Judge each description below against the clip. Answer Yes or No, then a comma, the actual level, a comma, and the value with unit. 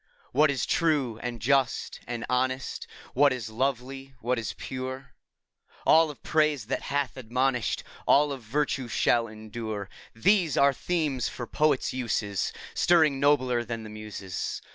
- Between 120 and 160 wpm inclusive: Yes, average, 150 wpm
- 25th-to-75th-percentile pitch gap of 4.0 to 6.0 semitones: No, average, 3.5 semitones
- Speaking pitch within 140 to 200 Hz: No, low, 130 Hz